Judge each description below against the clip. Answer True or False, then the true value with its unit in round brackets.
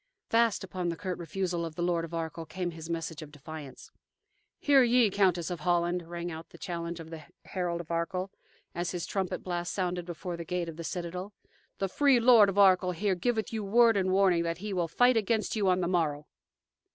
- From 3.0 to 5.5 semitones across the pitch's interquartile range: False (2.6 semitones)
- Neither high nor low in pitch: True (180 Hz)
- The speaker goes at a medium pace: False (210 wpm)